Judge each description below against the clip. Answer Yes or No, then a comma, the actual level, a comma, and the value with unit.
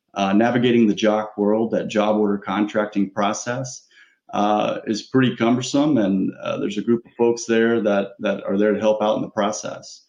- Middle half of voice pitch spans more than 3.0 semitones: No, narrow, 2.4 semitones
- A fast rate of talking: No, average, 190 wpm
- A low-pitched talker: Yes, low, 105 Hz